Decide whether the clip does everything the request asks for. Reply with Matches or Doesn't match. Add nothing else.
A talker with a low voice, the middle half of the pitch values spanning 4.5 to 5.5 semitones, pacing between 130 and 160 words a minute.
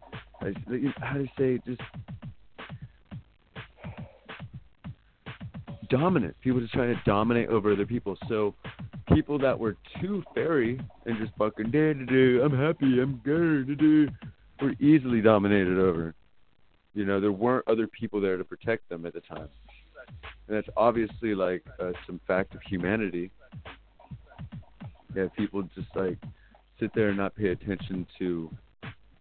Matches